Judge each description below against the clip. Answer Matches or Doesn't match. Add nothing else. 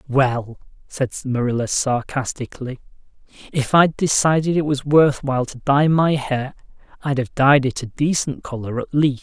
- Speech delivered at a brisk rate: Doesn't match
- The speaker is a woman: Doesn't match